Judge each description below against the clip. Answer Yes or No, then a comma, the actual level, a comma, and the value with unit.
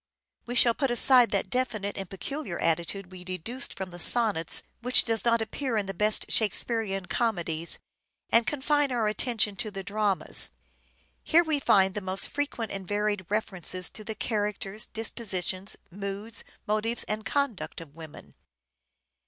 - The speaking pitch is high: Yes, high, 210 Hz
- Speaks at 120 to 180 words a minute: Yes, average, 155 wpm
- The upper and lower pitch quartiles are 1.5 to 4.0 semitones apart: Yes, average, 3.7 semitones